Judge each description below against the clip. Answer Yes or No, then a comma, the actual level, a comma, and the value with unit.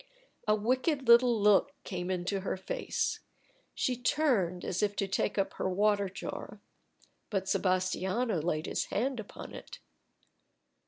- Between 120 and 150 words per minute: Yes, average, 140 wpm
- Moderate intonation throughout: Yes, average, 4.1 semitones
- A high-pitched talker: Yes, high, 200 Hz